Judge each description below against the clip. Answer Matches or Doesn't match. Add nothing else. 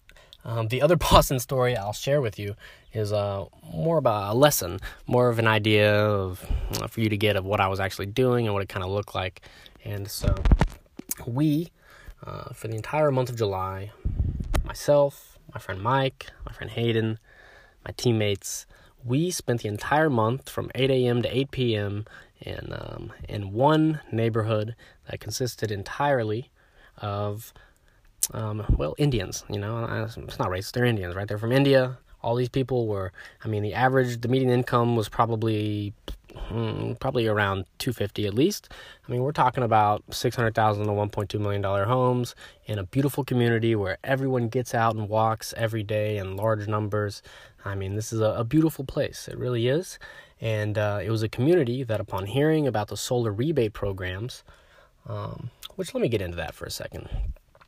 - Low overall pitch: Matches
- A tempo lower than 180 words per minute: Doesn't match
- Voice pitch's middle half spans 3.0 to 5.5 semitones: Matches